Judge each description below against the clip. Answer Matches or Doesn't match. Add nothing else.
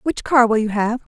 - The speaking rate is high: Matches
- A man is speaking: Doesn't match